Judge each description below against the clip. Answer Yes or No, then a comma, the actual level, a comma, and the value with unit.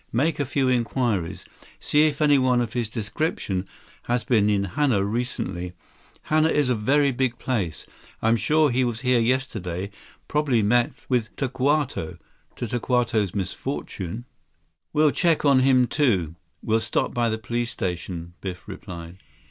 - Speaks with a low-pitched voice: Yes, low, 120 Hz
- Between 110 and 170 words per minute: Yes, average, 145 wpm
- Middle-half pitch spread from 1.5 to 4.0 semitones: No, average, 4.7 semitones